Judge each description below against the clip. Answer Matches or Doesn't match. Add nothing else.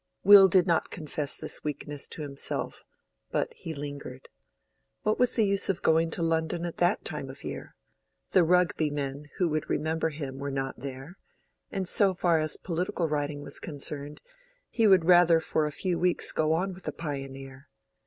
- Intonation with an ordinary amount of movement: Matches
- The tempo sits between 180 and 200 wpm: Matches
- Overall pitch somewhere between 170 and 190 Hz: Doesn't match